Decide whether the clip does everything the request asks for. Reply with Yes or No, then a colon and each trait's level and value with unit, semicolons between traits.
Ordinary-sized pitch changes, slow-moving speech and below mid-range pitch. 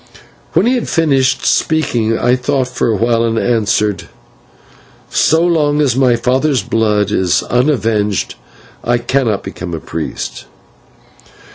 Yes: average, 4.3 semitones; slow, 130 wpm; low, 120 Hz